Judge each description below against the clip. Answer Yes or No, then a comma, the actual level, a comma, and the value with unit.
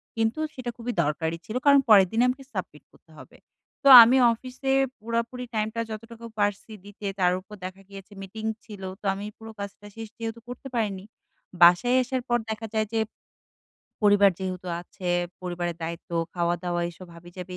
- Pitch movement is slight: No, average, 4.1 semitones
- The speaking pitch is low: No, high, 210 Hz